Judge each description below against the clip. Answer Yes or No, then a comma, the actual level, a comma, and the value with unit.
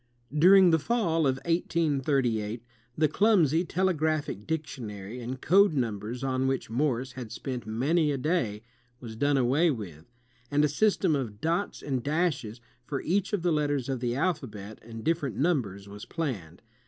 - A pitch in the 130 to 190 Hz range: Yes, medium, 140 Hz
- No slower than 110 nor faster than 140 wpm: No, average, 160 wpm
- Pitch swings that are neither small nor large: No, wide, 5.7 semitones